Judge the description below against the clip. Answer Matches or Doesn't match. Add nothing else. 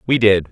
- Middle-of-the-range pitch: Doesn't match